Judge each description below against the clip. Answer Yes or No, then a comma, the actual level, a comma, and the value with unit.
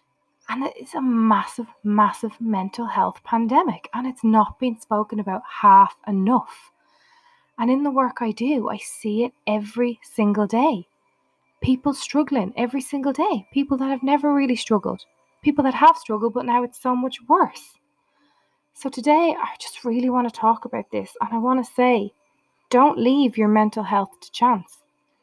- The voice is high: Yes, high, 245 Hz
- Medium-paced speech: Yes, average, 170 wpm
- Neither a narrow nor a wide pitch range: Yes, average, 4.0 semitones